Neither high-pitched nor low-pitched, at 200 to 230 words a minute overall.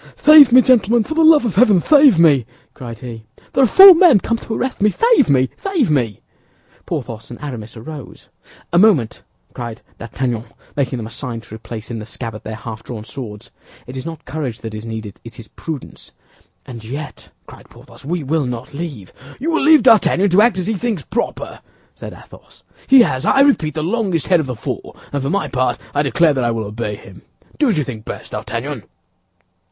Yes: medium, 145 Hz; fast, 205 wpm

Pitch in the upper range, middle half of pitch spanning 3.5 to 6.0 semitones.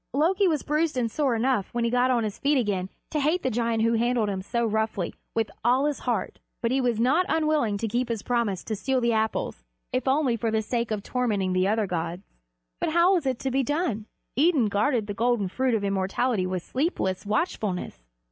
Yes: high, 235 Hz; average, 4.2 semitones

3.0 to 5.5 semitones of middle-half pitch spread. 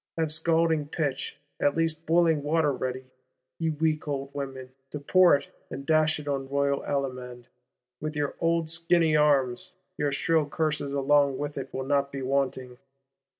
No: narrow, 2.6 semitones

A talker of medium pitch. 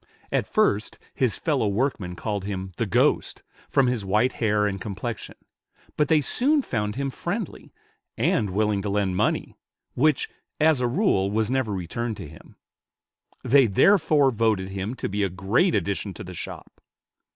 No: low, 110 Hz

